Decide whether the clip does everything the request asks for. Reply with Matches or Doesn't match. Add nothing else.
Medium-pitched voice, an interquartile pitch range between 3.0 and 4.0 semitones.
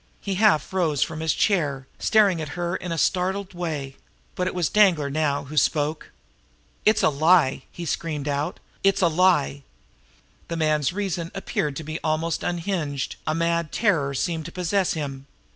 Matches